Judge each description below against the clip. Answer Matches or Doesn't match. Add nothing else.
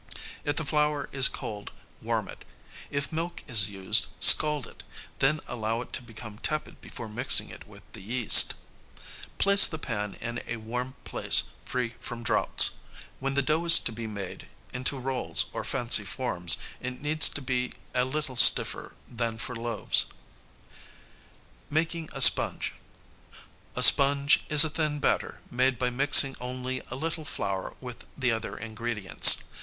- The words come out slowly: Doesn't match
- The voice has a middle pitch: Doesn't match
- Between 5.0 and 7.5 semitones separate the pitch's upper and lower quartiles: Doesn't match